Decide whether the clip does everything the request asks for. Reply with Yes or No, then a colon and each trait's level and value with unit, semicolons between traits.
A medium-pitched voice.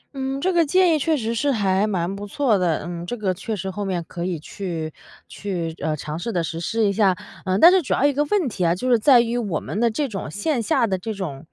No: high, 205 Hz